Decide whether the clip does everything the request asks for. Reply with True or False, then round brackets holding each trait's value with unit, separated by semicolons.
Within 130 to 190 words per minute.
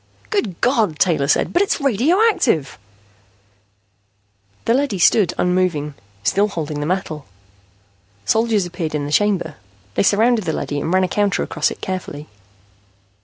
True (140 wpm)